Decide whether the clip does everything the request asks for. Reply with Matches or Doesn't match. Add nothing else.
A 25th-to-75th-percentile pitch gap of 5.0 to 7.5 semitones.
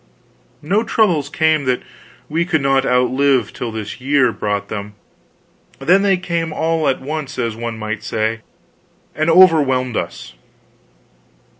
Matches